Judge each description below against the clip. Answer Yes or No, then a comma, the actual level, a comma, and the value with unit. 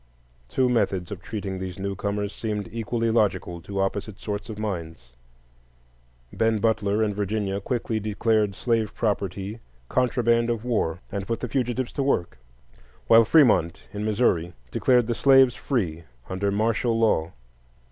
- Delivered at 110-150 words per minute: Yes, average, 140 wpm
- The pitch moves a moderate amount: Yes, average, 3.0 semitones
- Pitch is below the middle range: Yes, low, 105 Hz